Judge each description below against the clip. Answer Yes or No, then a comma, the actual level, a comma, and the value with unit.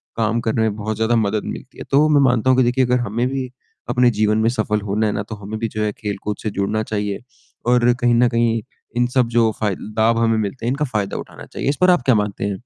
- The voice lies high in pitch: No, low, 115 Hz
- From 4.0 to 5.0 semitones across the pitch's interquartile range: No, narrow, 2.5 semitones